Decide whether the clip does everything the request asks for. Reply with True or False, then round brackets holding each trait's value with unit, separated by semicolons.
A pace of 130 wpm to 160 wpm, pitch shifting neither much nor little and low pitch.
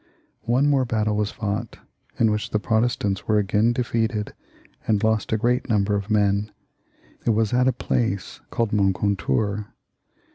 False (150 wpm; 2.2 semitones; 105 Hz)